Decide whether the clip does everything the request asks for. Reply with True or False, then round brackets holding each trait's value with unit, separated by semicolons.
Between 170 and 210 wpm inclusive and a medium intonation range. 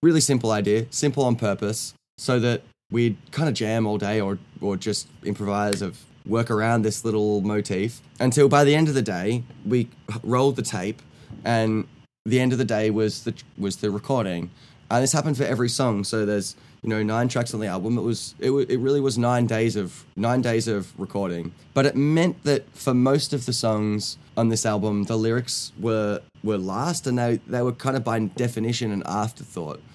True (200 wpm; 3.4 semitones)